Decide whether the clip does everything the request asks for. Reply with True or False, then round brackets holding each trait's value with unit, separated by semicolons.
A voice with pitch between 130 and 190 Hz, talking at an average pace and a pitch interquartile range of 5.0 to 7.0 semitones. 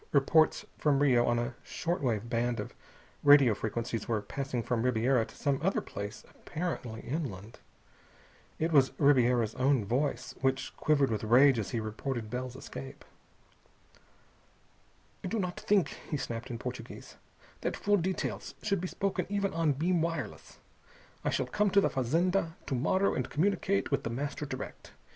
True (135 Hz; 160 wpm; 5.5 semitones)